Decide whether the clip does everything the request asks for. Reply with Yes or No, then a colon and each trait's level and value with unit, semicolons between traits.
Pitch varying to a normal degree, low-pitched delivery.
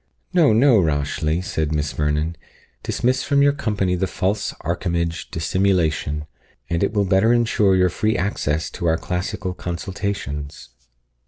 Yes: average, 4.6 semitones; very low, 90 Hz